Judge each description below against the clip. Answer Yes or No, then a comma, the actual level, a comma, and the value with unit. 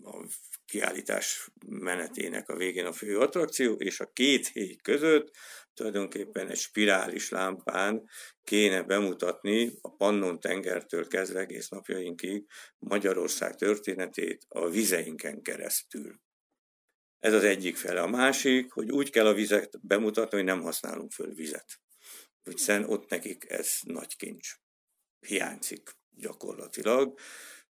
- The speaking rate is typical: Yes, average, 115 wpm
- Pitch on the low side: Yes, low, 105 Hz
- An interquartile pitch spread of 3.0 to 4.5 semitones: No, narrow, 2.5 semitones